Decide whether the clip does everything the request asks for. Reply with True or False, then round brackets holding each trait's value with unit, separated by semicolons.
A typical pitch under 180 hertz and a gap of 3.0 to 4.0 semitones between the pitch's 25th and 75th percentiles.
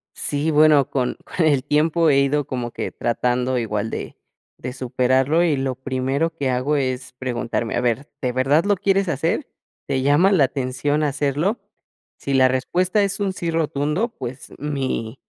True (140 Hz; 3.5 semitones)